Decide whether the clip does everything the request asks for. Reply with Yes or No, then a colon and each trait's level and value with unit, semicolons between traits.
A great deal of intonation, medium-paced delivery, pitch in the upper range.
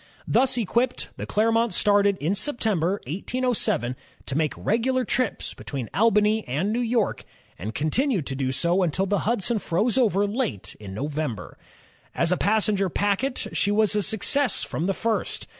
Yes: wide, 5.7 semitones; average, 160 wpm; high, 205 Hz